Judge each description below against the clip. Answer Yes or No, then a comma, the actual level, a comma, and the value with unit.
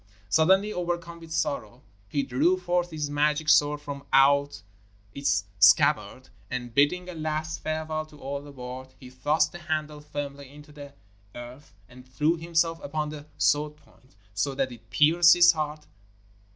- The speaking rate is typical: Yes, average, 160 wpm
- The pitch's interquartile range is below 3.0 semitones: Yes, narrow, 2.5 semitones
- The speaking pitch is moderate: Yes, medium, 150 Hz